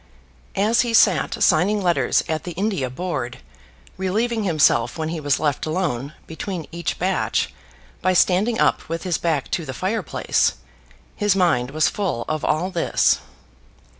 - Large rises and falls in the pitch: No, average, 3.8 semitones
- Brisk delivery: No, average, 155 wpm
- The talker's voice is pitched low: No, medium, 170 Hz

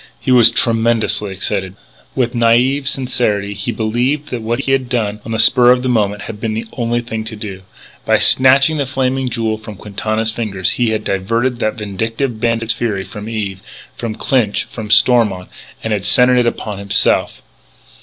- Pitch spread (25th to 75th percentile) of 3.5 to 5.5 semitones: No, average, 2.7 semitones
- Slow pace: No, average, 185 wpm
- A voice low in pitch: Yes, low, 115 Hz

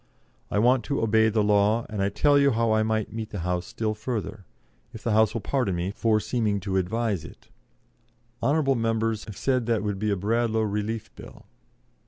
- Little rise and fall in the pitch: Yes, narrow, 2.0 semitones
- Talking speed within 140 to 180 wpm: No, average, 200 wpm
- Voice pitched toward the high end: No, low, 110 Hz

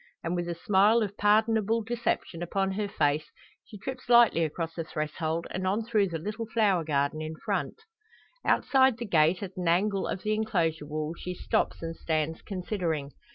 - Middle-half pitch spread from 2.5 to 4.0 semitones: No, average, 4.8 semitones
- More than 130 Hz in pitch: Yes, medium, 185 Hz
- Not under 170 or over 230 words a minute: Yes, average, 180 wpm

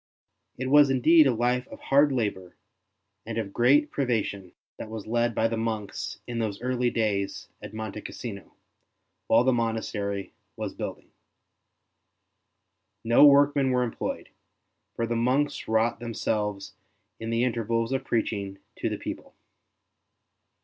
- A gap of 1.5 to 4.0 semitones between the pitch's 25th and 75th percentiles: Yes, narrow, 2.6 semitones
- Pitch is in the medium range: No, low, 115 Hz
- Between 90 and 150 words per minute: Yes, average, 140 wpm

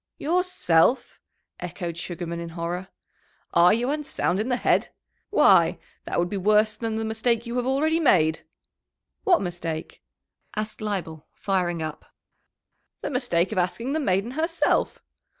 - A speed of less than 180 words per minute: Yes, average, 140 wpm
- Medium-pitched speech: No, high, 210 Hz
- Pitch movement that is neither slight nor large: No, wide, 6.2 semitones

